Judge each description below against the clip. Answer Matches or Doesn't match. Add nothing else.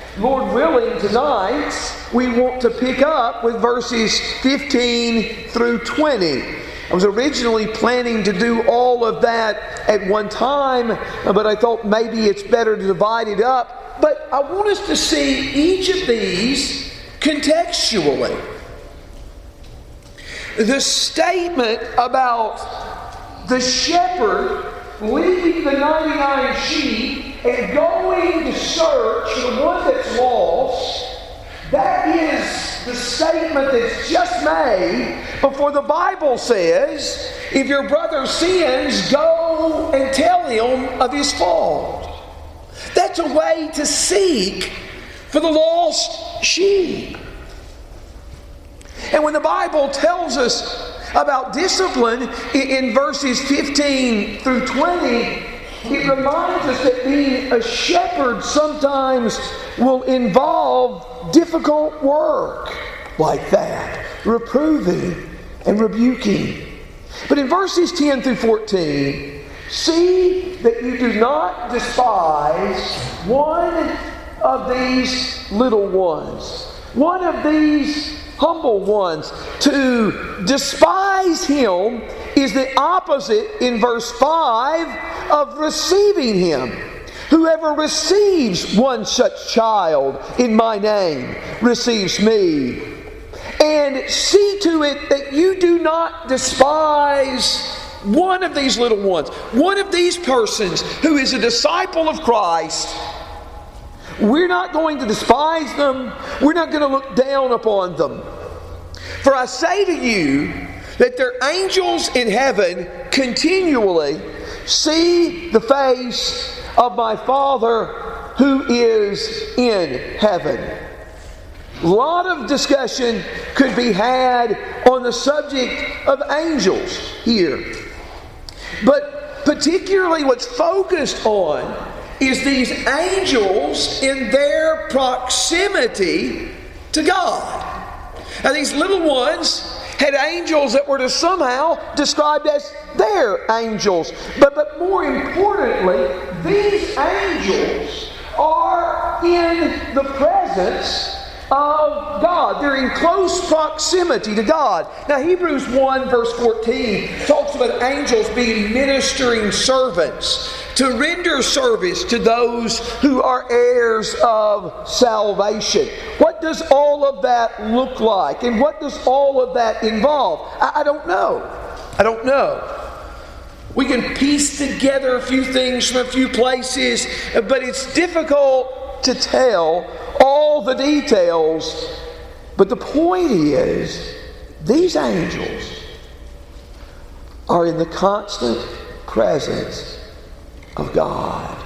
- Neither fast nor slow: Doesn't match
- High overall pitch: Matches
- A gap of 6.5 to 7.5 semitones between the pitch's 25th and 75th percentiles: Doesn't match